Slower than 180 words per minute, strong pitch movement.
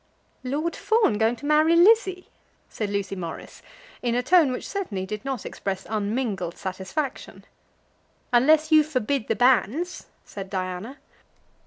Yes: slow, 135 wpm; wide, 7.4 semitones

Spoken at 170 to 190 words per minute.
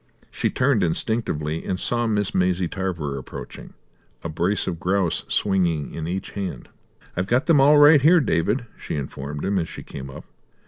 Yes: average, 175 wpm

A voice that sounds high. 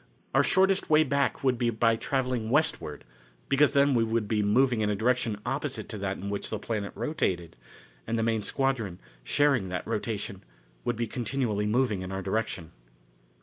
No: low, 115 Hz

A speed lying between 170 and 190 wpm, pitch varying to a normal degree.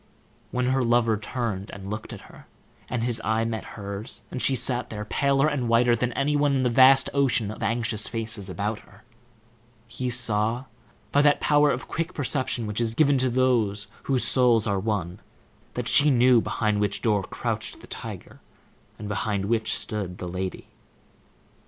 Yes: average, 175 wpm; average, 3.5 semitones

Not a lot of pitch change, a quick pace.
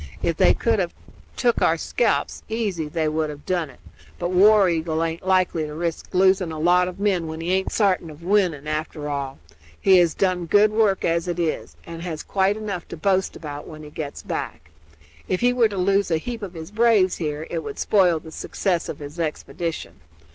No: average, 3.6 semitones; fast, 210 wpm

